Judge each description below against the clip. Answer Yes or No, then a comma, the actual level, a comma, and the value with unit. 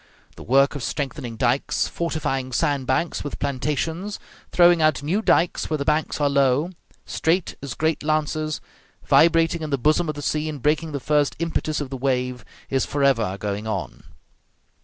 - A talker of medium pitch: Yes, medium, 145 Hz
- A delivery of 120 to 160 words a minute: No, average, 170 wpm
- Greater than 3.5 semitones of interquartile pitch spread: No, average, 3.1 semitones